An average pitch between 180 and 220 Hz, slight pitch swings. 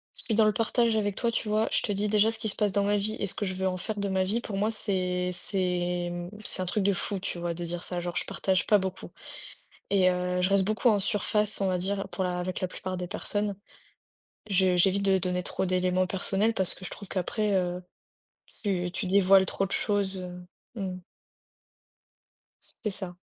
Yes: high, 190 Hz; narrow, 2.2 semitones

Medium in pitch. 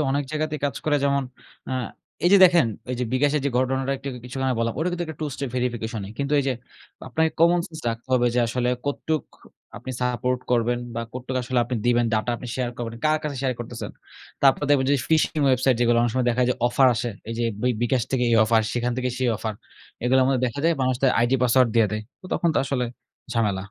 No: low, 130 Hz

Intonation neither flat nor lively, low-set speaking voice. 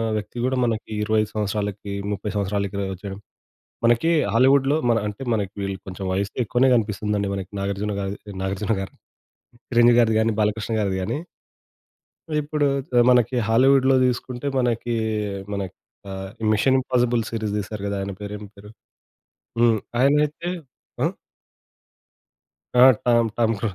Yes: average, 3.4 semitones; low, 110 Hz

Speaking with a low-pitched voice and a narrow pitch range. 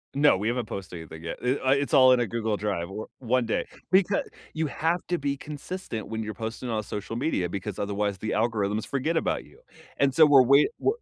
No: low, 115 Hz; average, 5.1 semitones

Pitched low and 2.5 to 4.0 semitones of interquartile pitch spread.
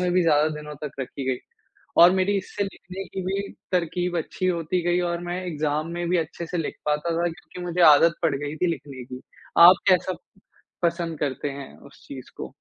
No: medium, 170 Hz; average, 3.3 semitones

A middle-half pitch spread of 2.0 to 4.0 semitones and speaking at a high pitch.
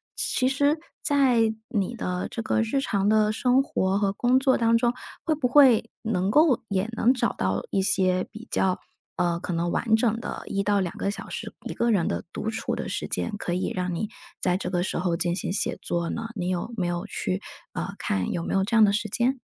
No: average, 4.5 semitones; high, 210 Hz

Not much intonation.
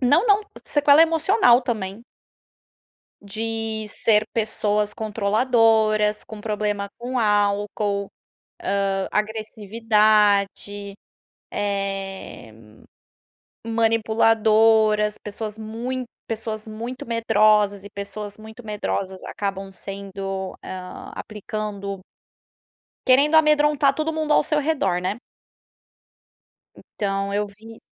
Yes: narrow, 2.2 semitones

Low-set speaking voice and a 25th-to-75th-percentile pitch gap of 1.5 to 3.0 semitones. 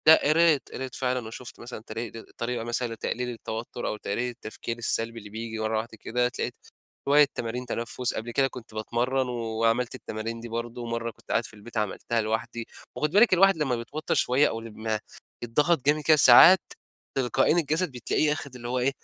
Yes: low, 120 Hz; average, 2.7 semitones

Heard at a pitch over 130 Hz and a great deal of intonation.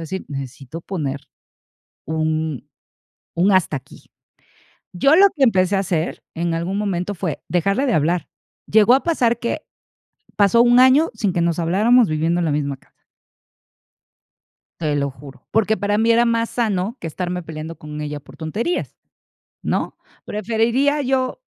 Yes: medium, 185 Hz; wide, 6.5 semitones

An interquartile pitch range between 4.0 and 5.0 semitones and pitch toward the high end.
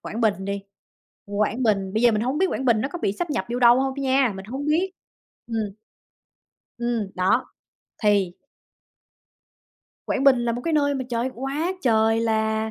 No: average, 3.6 semitones; high, 235 Hz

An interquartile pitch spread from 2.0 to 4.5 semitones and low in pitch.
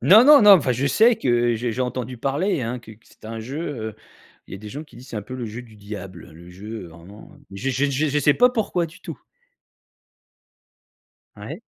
No: average, 5.3 semitones; low, 125 Hz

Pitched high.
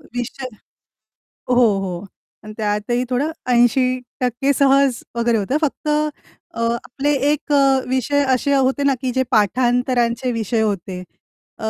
Yes: very high, 250 Hz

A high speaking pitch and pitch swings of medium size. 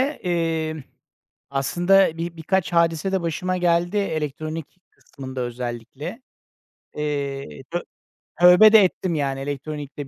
No: medium, 160 Hz; average, 4.1 semitones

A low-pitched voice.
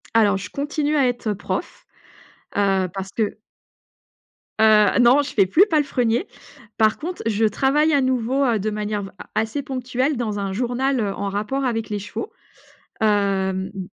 No: high, 225 Hz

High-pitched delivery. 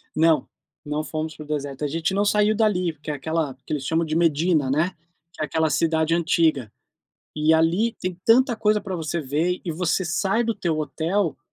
No: medium, 165 Hz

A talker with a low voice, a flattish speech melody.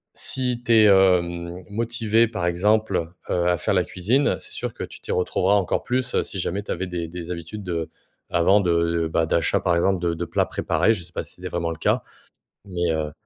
No: very low, 90 Hz; average, 3.3 semitones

